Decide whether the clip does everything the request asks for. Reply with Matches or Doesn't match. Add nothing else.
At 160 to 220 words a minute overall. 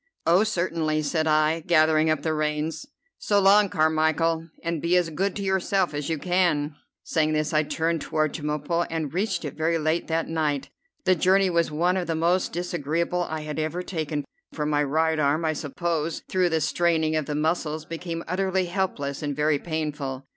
Matches